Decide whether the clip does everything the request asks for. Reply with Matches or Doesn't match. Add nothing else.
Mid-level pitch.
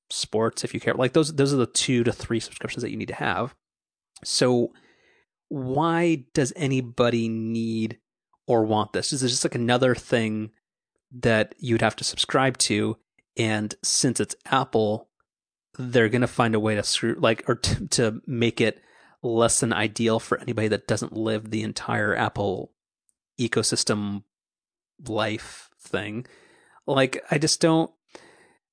Doesn't match